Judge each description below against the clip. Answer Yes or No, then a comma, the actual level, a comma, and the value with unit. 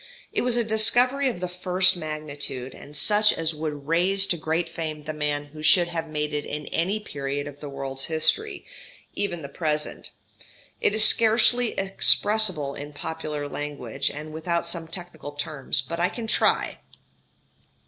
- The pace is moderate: Yes, average, 165 wpm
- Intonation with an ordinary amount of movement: Yes, average, 4.5 semitones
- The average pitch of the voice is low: No, medium, 160 Hz